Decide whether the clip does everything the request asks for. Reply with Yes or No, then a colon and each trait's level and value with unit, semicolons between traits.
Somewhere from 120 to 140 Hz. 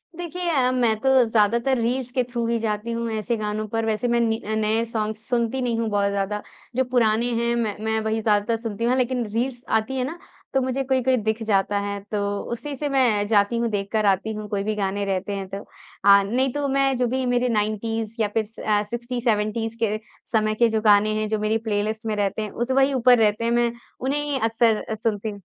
No: high, 225 Hz